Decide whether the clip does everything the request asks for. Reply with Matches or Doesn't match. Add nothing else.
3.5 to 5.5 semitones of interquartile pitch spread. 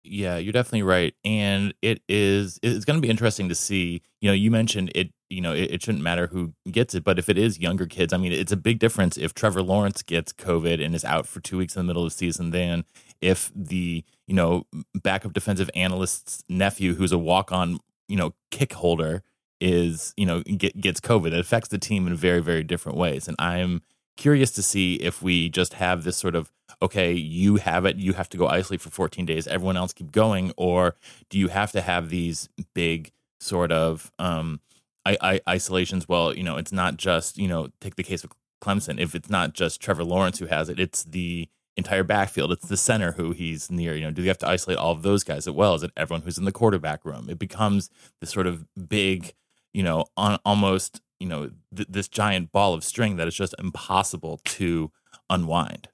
Doesn't match